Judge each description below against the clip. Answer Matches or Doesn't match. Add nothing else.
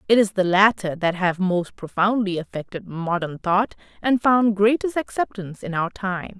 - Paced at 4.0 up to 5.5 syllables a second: Matches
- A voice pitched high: Matches